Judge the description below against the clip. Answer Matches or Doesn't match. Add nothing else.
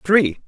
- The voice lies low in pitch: Doesn't match